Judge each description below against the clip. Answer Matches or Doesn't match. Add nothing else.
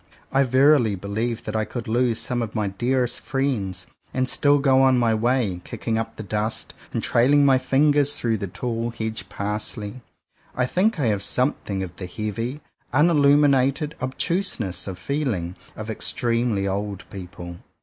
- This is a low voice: Matches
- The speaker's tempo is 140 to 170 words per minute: Matches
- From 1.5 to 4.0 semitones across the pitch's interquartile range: Doesn't match